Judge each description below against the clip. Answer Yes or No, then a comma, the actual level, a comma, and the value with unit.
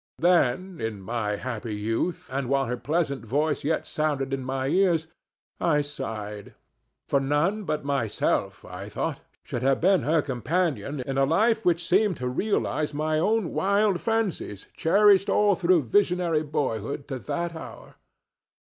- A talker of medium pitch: Yes, medium, 150 Hz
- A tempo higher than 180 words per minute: No, average, 150 wpm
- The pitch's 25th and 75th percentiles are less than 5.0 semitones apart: No, wide, 5.6 semitones